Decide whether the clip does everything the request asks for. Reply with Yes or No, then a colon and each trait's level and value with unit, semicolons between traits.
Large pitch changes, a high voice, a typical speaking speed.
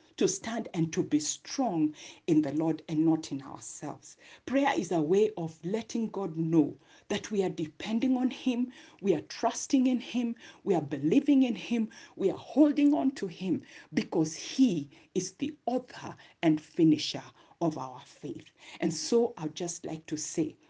Yes: wide, 8.7 semitones; high, 200 Hz; average, 175 wpm